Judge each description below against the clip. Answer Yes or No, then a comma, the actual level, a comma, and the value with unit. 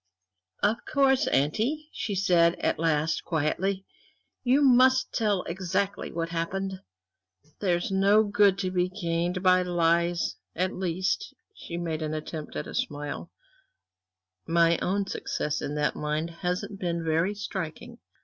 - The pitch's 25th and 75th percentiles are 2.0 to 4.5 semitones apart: Yes, average, 3.1 semitones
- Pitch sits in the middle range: Yes, medium, 180 Hz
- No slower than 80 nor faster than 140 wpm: Yes, slow, 135 wpm